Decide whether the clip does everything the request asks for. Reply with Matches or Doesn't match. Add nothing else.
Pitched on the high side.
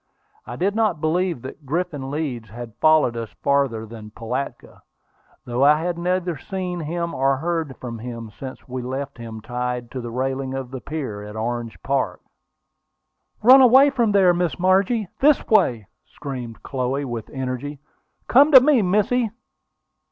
Doesn't match